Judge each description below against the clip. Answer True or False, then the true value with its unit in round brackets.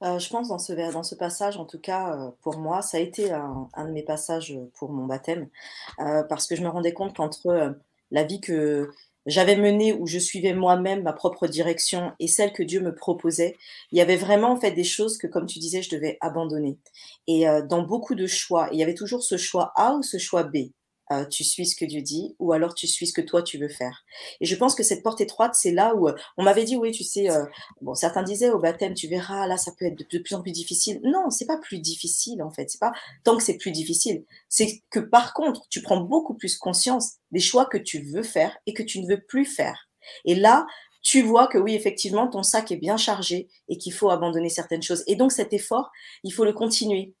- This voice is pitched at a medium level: True (180 Hz)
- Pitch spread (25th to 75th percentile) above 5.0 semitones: False (4.4 semitones)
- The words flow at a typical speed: False (250 wpm)